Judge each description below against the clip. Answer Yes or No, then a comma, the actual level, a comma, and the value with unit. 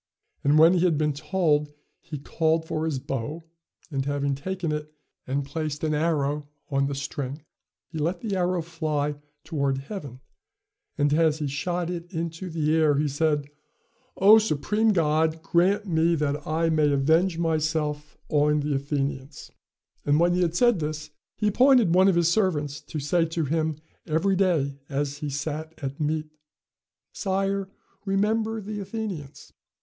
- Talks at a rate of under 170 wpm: Yes, average, 160 wpm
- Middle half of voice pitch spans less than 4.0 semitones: Yes, average, 3.2 semitones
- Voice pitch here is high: No, medium, 155 Hz